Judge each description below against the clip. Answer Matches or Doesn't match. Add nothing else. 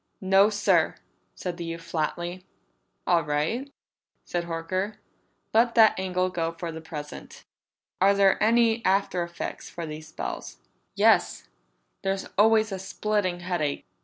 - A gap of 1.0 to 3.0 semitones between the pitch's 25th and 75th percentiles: Doesn't match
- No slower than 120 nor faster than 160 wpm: Matches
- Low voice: Doesn't match